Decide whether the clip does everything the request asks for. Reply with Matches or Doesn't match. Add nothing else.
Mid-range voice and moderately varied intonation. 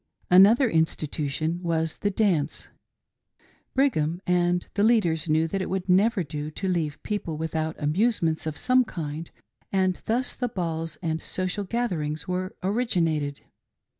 Matches